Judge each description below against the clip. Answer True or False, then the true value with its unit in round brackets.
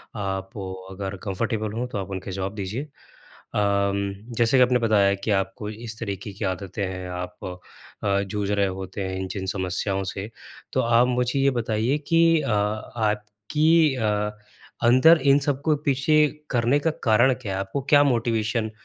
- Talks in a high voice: False (105 Hz)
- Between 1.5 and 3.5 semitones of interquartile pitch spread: False (4.2 semitones)